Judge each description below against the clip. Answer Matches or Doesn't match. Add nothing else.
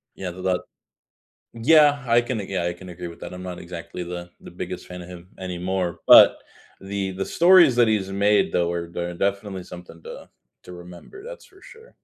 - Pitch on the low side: Matches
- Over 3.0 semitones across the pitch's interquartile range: Matches